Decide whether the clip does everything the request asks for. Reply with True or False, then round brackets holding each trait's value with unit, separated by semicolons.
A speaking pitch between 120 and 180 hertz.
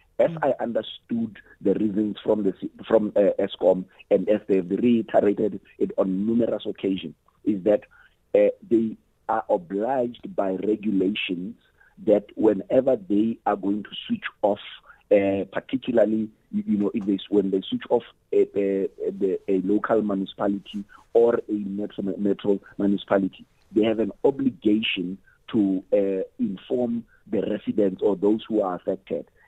False (105 Hz)